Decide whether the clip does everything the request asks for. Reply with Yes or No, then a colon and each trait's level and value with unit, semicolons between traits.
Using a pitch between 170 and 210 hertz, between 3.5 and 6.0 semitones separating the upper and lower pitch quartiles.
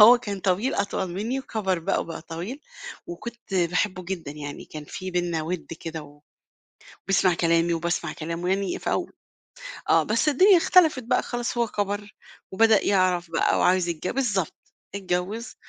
Yes: medium, 185 Hz; average, 4.3 semitones